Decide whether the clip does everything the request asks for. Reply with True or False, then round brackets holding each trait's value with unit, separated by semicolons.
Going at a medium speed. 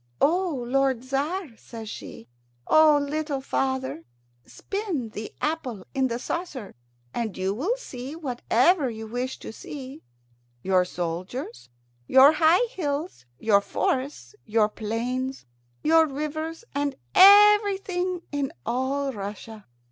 False (115 wpm)